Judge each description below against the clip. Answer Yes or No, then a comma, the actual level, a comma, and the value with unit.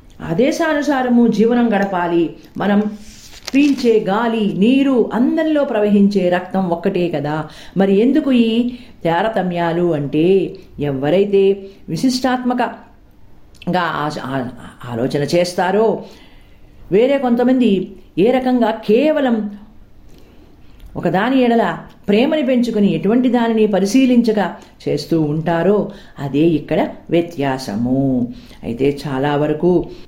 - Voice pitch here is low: No, high, 200 Hz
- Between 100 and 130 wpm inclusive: No, average, 80 wpm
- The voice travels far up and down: Yes, wide, 6.1 semitones